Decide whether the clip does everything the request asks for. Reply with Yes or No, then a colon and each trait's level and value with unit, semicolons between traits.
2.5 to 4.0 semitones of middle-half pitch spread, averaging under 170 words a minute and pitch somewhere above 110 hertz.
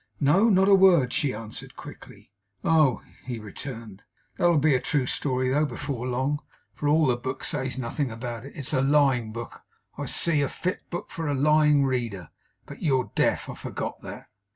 No: average, 3.5 semitones; average, 185 wpm; low, 135 Hz